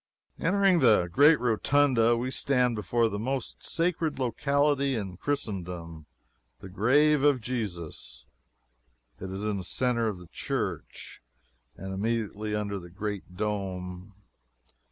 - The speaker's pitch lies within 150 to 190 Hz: No, low, 110 Hz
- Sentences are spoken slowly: Yes, slow, 125 wpm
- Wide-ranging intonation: Yes, wide, 6.0 semitones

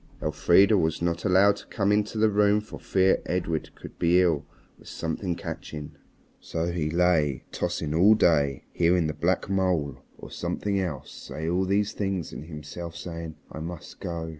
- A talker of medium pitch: No, very low, 85 Hz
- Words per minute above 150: Yes, average, 170 wpm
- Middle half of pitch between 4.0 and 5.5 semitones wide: No, average, 3.4 semitones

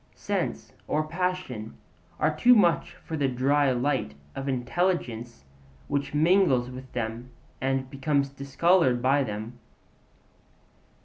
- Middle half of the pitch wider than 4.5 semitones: No, average, 3.8 semitones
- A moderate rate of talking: No, slow, 115 wpm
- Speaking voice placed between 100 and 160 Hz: Yes, low, 135 Hz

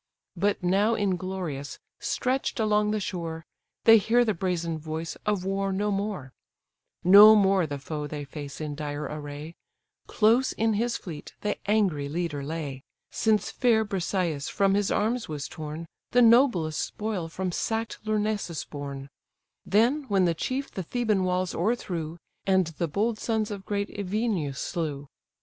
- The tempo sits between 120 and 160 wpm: Yes, average, 150 wpm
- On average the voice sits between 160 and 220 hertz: Yes, high, 190 Hz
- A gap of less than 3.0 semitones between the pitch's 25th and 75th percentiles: No, average, 5.2 semitones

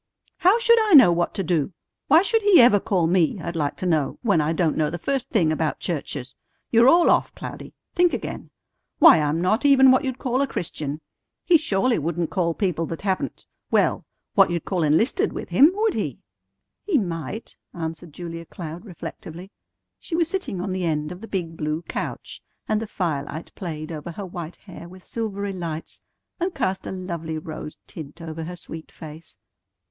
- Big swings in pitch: Yes, wide, 5.9 semitones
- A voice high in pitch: No, medium, 175 Hz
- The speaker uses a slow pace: No, average, 190 wpm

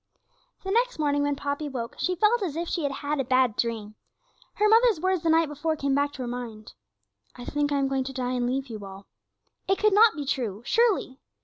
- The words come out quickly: Yes, fast, 230 wpm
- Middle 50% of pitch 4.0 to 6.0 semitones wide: Yes, wide, 5.4 semitones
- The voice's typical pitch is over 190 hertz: Yes, very high, 285 Hz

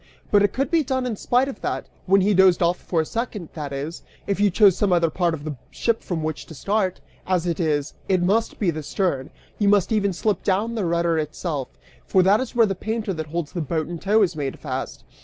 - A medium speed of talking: No, fast, 245 wpm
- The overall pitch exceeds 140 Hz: Yes, medium, 185 Hz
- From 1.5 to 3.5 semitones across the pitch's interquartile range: No, average, 4.3 semitones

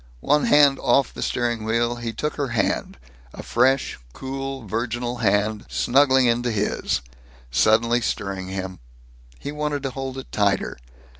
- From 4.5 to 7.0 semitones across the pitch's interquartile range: No, average, 3.7 semitones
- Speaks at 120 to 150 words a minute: Yes, average, 145 wpm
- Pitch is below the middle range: Yes, low, 120 Hz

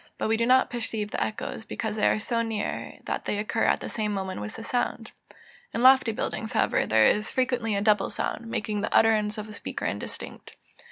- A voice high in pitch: Yes, high, 220 Hz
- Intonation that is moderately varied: No, narrow, 1.7 semitones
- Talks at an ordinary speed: No, fast, 215 wpm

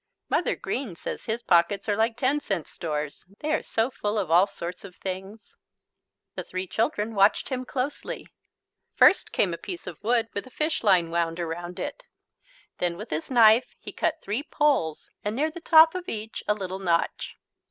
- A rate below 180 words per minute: No, average, 185 wpm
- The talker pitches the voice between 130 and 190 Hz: No, high, 210 Hz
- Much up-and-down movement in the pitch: Yes, wide, 6.2 semitones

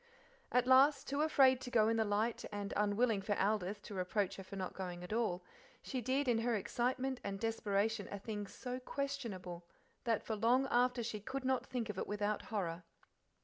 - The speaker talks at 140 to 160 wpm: No, average, 195 wpm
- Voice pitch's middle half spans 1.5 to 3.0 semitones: No, average, 3.9 semitones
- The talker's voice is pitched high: Yes, high, 220 Hz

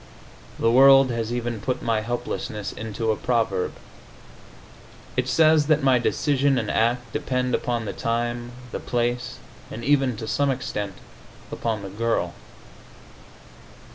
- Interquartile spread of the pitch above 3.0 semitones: No, narrow, 2.4 semitones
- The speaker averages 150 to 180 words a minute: No, slow, 135 wpm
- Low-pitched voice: Yes, low, 120 Hz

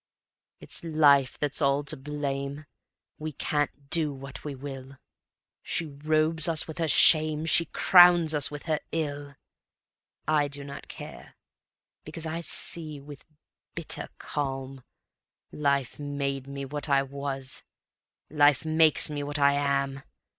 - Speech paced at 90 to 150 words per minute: Yes, slow, 135 wpm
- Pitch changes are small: Yes, narrow, 1.9 semitones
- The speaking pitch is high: No, medium, 145 Hz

